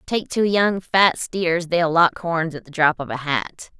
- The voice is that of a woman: Yes, female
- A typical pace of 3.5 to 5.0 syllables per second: Yes, 3.9 syllables/s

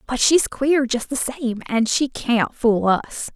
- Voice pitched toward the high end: Yes, very high, 250 Hz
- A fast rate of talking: No, average, 195 wpm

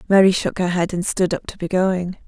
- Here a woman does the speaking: Yes, female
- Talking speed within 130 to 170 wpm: No, fast, 265 wpm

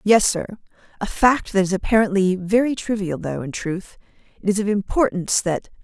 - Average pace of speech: Yes, average, 175 wpm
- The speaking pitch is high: Yes, high, 200 Hz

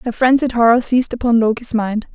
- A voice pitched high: Yes, high, 235 Hz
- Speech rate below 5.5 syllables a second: No, 5.9 syllables/s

